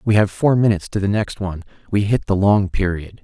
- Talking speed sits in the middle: No, fast, 225 wpm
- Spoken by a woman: No, male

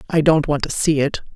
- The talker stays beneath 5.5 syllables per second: No, 5.6 syllables/s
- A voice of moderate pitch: Yes, medium, 150 Hz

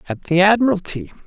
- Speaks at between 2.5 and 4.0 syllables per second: No, 6.1 syllables/s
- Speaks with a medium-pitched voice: Yes, medium, 180 Hz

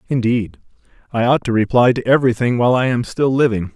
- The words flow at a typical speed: Yes, average, 190 wpm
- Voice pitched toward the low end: Yes, low, 120 Hz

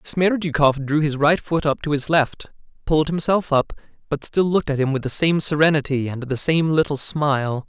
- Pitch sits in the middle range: Yes, medium, 150 Hz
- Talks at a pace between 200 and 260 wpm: Yes, fast, 205 wpm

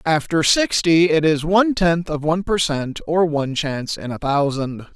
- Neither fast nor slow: Yes, average, 195 wpm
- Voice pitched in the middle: Yes, medium, 160 Hz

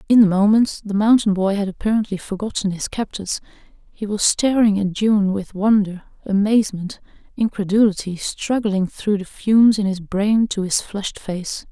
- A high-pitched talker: Yes, high, 205 Hz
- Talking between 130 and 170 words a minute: Yes, average, 155 wpm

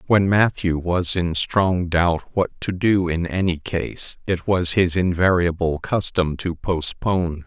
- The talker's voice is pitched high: No, very low, 90 Hz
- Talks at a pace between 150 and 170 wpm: Yes, average, 155 wpm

